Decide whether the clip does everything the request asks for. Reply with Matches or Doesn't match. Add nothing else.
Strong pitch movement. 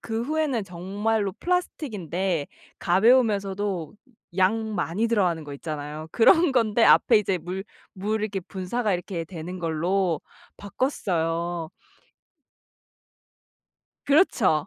Doesn't match